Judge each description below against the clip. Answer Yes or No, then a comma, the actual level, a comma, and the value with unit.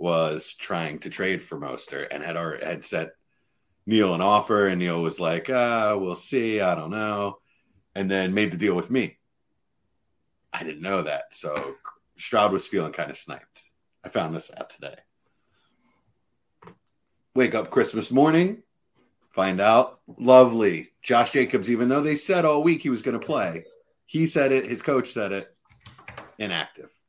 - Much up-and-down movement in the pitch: Yes, wide, 6.3 semitones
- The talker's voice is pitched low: Yes, low, 120 Hz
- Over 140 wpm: Yes, average, 165 wpm